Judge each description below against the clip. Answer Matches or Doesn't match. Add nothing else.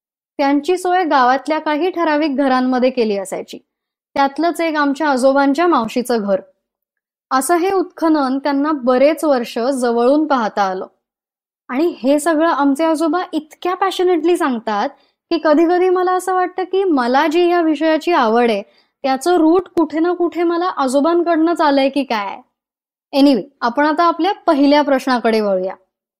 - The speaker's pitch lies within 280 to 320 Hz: Matches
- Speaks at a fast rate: Matches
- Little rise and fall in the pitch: Doesn't match